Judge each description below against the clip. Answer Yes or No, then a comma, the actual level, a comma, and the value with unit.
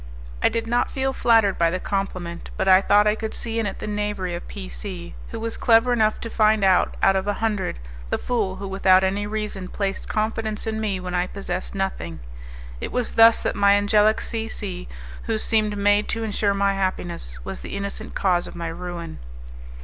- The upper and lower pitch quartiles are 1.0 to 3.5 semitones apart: Yes, average, 2.7 semitones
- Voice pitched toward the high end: Yes, high, 200 Hz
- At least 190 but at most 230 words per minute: Yes, fast, 205 wpm